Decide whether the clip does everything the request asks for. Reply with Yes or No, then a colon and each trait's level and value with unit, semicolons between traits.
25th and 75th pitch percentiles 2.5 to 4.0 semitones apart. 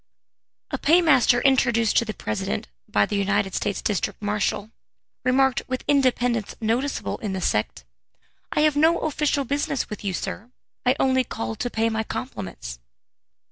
No: average, 4.8 semitones